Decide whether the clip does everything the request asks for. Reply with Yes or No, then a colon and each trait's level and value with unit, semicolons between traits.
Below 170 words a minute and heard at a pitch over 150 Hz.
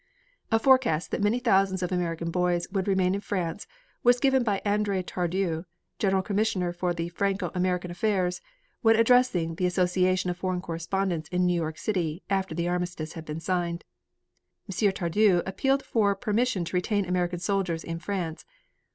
Yes: average, 160 wpm; medium, 185 Hz